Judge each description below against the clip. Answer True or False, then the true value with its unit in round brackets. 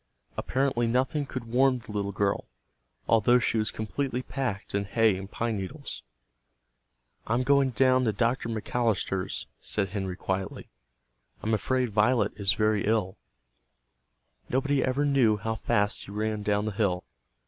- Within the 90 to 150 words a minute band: True (145 wpm)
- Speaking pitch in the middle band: False (110 Hz)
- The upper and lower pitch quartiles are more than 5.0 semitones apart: False (3.9 semitones)